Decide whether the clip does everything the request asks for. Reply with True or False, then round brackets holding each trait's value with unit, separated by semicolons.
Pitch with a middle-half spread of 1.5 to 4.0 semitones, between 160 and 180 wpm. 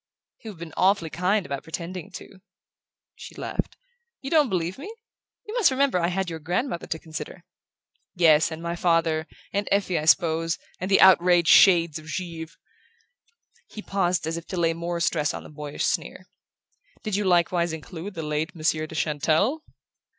True (2.8 semitones; 170 wpm)